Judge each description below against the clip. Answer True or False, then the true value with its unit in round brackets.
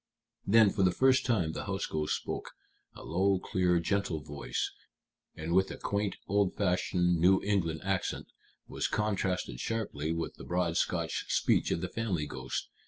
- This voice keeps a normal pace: True (165 wpm)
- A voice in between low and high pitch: False (90 Hz)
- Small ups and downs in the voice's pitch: False (3.3 semitones)